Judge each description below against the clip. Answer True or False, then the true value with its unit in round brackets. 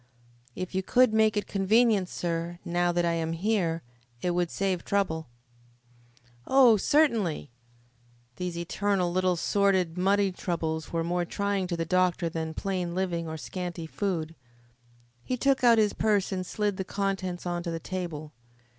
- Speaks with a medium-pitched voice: True (180 Hz)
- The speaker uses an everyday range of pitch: True (3.0 semitones)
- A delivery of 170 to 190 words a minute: False (160 wpm)